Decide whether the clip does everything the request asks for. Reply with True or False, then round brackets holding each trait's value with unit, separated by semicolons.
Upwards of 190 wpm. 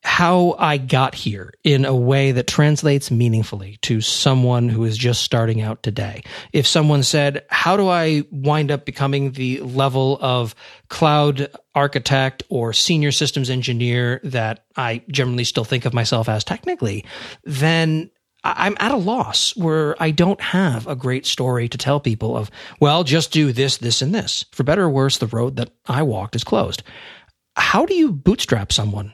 False (175 wpm)